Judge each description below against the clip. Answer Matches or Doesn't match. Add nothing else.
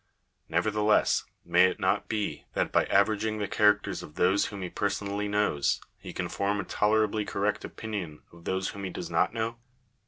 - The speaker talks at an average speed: Matches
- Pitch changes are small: Matches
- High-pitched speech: Doesn't match